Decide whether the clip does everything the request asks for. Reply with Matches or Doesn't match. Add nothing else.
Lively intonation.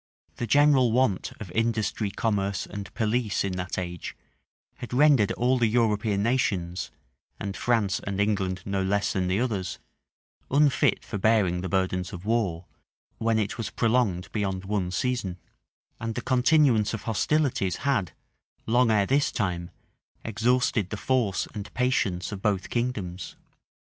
Doesn't match